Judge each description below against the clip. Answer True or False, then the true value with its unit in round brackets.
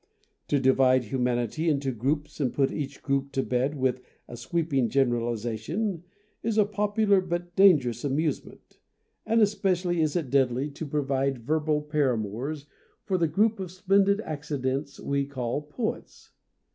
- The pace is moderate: True (145 wpm)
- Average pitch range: True (5.0 semitones)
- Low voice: False (145 Hz)